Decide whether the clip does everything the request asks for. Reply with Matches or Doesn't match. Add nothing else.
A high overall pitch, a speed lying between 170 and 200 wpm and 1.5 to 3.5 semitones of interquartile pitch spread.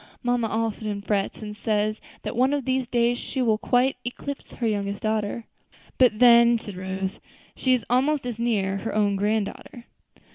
Matches